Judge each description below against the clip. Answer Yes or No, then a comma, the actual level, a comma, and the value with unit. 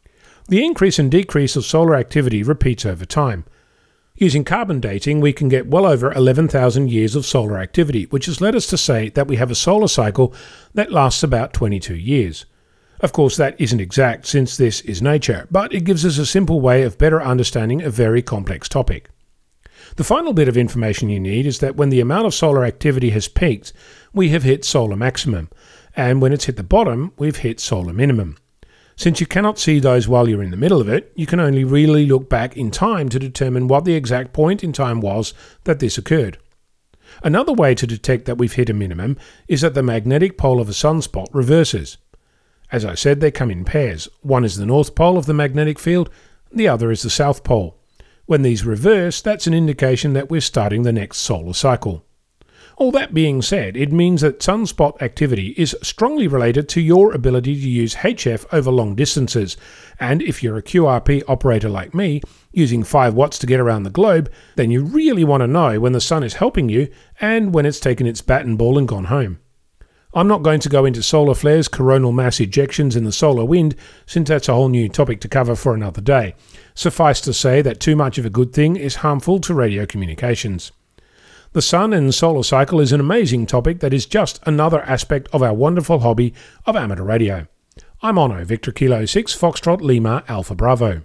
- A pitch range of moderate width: Yes, average, 4.7 semitones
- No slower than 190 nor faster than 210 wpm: Yes, fast, 205 wpm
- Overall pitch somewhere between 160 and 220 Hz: No, low, 135 Hz